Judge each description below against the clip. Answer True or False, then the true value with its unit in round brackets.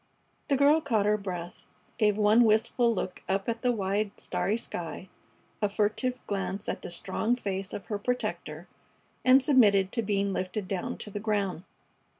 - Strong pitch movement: False (3.2 semitones)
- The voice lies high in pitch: True (210 Hz)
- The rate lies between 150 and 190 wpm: True (165 wpm)